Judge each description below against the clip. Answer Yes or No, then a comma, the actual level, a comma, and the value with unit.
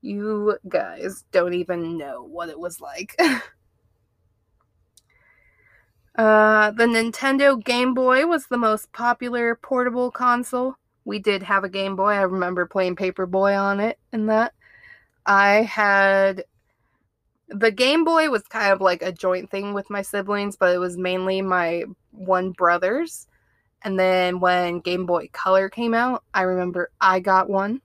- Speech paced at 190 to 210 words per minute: No, average, 150 wpm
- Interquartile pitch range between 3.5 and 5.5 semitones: Yes, average, 3.9 semitones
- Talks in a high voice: Yes, high, 195 Hz